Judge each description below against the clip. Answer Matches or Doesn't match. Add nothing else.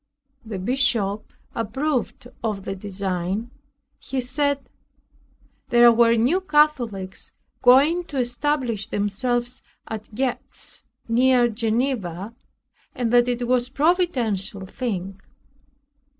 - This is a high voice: Matches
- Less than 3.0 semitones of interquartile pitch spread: Doesn't match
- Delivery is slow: Matches